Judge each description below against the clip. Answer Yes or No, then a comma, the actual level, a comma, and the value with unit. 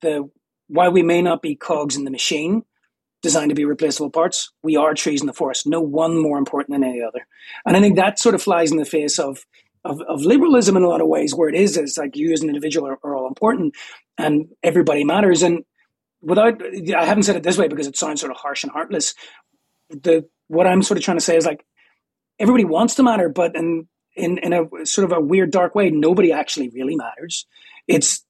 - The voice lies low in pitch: No, medium, 165 Hz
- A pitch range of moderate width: Yes, average, 4.0 semitones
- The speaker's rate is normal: No, fast, 230 wpm